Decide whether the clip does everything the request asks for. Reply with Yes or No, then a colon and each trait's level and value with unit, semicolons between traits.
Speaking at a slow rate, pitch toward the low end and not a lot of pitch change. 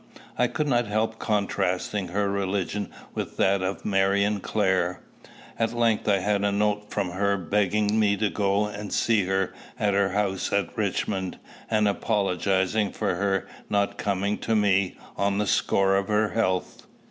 No: average, 160 wpm; low, 100 Hz; narrow, 1.5 semitones